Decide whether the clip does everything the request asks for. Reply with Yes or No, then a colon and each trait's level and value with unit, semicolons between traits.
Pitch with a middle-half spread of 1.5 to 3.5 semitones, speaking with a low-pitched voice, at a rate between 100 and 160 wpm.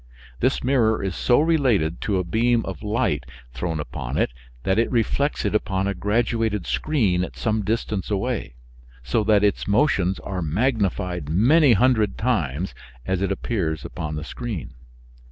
No: average, 4.3 semitones; low, 105 Hz; average, 155 wpm